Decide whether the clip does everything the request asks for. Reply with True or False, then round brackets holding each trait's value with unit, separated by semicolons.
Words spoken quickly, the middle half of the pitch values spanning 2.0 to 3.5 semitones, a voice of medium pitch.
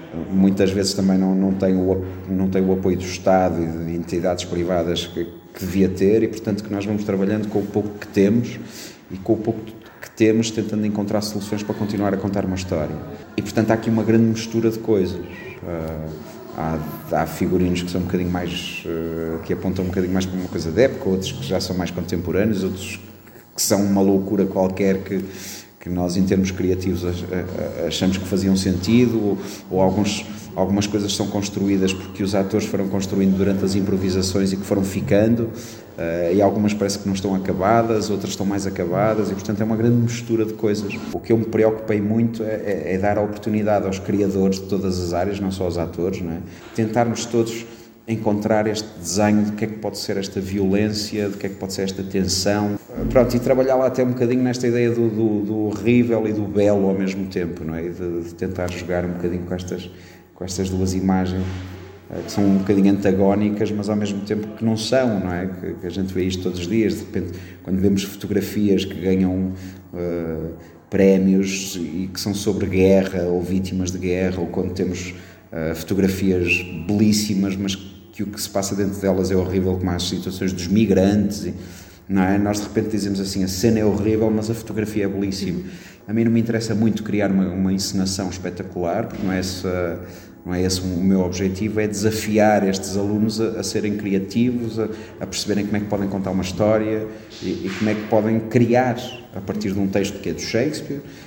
False (205 wpm; 2.4 semitones; 100 Hz)